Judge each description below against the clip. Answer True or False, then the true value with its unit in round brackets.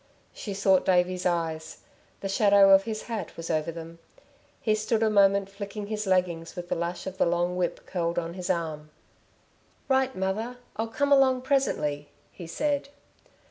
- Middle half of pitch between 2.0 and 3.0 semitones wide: False (4.0 semitones)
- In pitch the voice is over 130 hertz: True (190 Hz)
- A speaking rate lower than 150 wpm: False (170 wpm)